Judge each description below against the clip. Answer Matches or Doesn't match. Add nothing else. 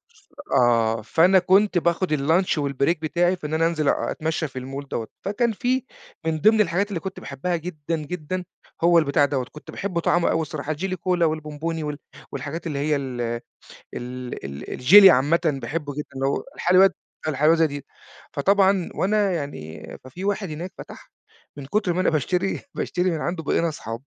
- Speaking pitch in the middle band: Matches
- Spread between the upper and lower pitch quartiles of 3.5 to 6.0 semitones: Matches